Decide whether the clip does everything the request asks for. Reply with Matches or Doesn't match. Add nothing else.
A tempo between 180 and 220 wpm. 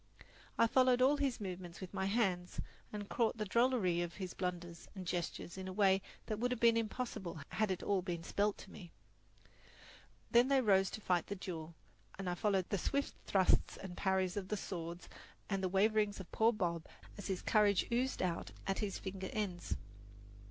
Matches